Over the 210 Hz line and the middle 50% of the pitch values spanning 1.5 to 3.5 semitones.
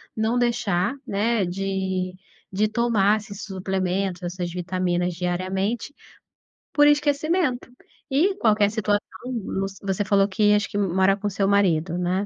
No: high, 195 Hz; average, 3.0 semitones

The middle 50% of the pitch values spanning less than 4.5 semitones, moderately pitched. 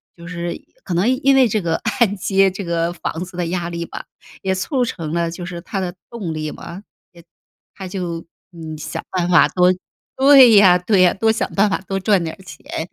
Yes: average, 2.9 semitones; medium, 180 Hz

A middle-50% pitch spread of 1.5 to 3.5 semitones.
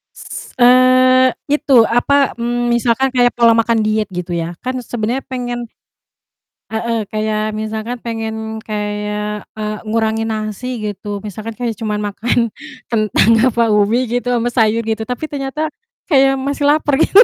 Yes: average, 2.8 semitones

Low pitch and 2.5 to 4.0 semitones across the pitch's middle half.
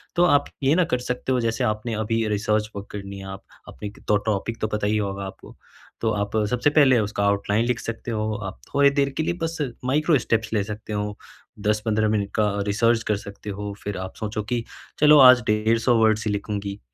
Yes: low, 110 Hz; average, 2.9 semitones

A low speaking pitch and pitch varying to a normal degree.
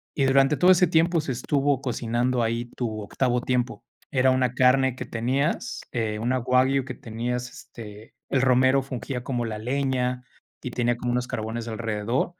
No: low, 125 Hz; narrow, 2.2 semitones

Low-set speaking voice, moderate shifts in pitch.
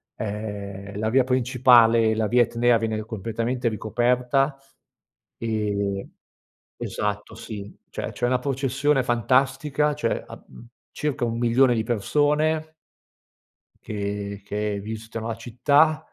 Yes: low, 115 Hz; average, 3.3 semitones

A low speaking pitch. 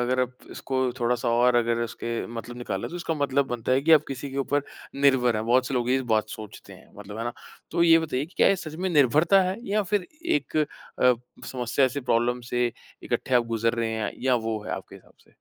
Yes: low, 125 Hz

